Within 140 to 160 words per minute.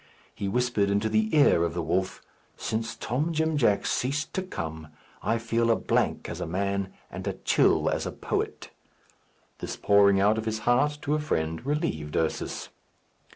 No: average, 175 wpm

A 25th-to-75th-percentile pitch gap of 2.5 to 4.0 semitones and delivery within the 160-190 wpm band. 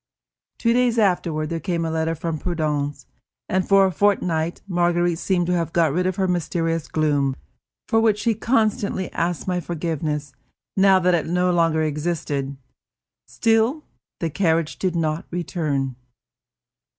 No: average, 3.0 semitones; average, 150 wpm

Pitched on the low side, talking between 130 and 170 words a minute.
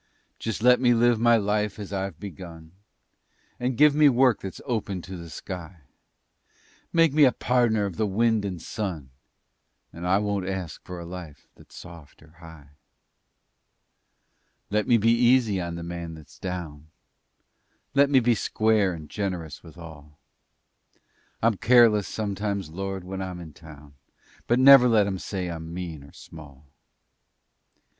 Yes: very low, 95 Hz; average, 150 wpm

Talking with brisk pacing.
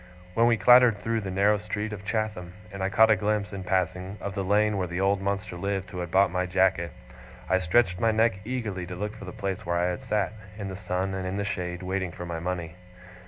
Yes: fast, 245 wpm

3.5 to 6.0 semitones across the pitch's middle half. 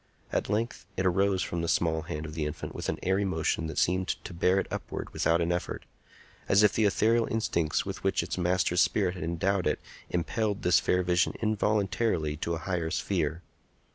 No: average, 3.0 semitones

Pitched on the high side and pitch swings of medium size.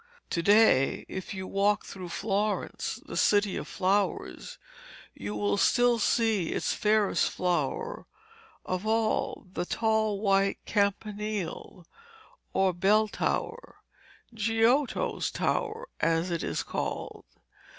Yes: high, 205 Hz; average, 3.1 semitones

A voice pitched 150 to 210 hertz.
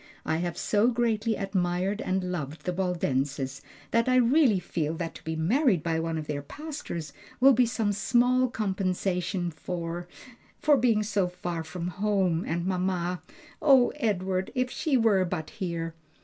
Yes: medium, 185 Hz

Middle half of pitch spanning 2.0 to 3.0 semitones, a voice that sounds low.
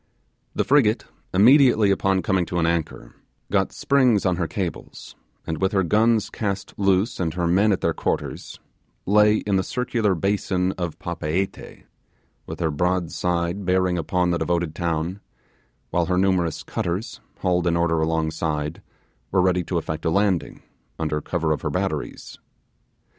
Yes: average, 2.7 semitones; very low, 90 Hz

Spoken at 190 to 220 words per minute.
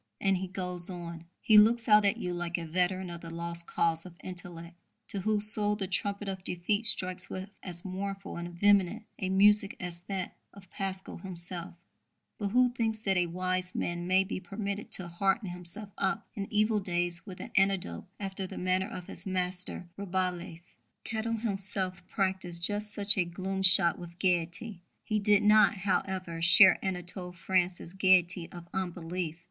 No: average, 175 wpm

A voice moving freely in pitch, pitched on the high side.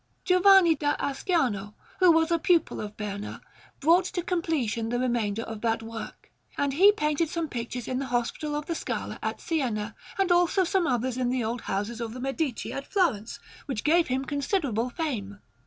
Yes: wide, 6.5 semitones; very high, 270 Hz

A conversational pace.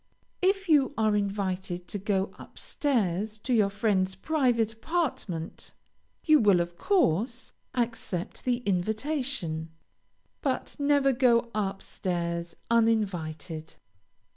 No: slow, 110 wpm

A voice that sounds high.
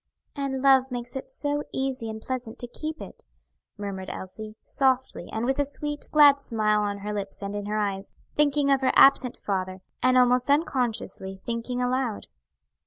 Yes: very high, 250 Hz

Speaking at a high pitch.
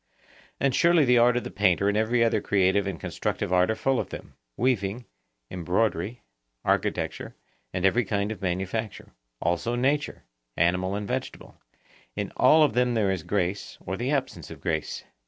No: low, 105 Hz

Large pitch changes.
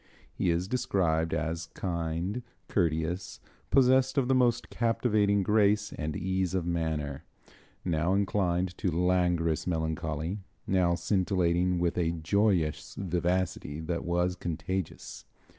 No: average, 3.0 semitones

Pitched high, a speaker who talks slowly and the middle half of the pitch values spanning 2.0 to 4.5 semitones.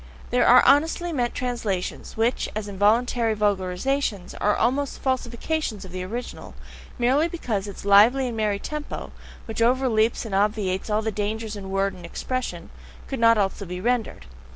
No: high, 220 Hz; average, 155 wpm; average, 3.8 semitones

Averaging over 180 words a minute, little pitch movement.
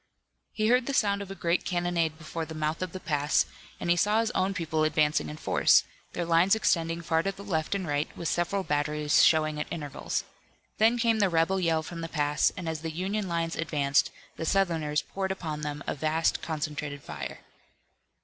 No: average, 200 wpm; average, 3.7 semitones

